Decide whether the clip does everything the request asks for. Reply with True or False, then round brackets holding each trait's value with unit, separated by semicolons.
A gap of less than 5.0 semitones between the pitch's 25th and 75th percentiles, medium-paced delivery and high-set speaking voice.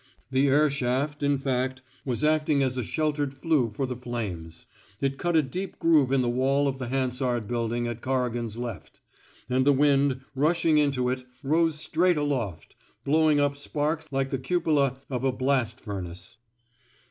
False (2.9 semitones; 170 wpm; 135 Hz)